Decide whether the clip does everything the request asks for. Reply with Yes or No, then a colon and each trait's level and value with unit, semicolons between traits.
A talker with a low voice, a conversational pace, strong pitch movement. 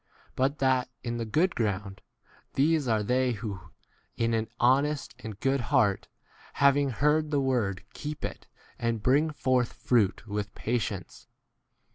No: low, 125 Hz; average, 145 wpm; average, 4.2 semitones